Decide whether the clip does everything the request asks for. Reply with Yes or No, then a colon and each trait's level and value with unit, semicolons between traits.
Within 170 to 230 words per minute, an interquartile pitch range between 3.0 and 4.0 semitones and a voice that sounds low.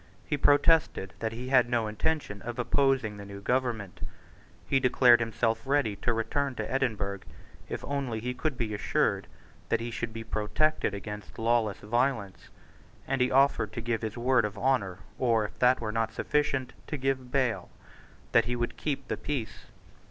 Yes: average, 175 wpm; average, 3.5 semitones; low, 120 Hz